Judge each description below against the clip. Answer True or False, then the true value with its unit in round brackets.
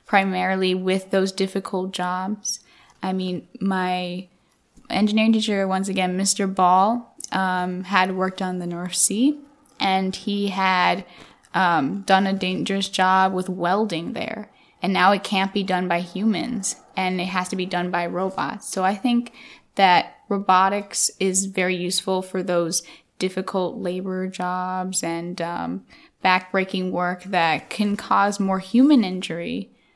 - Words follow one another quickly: False (140 wpm)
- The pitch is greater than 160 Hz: True (190 Hz)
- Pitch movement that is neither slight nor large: False (1.5 semitones)